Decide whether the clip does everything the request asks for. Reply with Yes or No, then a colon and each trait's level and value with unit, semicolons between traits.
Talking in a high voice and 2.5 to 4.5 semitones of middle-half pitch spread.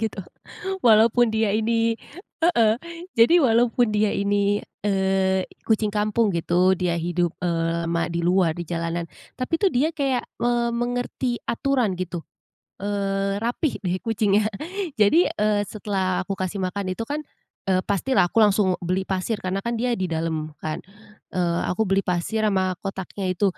Yes: high, 200 Hz; average, 3.7 semitones